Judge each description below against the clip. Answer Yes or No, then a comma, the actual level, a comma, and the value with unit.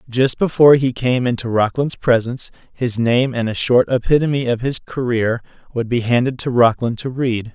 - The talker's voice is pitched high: No, low, 125 Hz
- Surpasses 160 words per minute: Yes, average, 185 wpm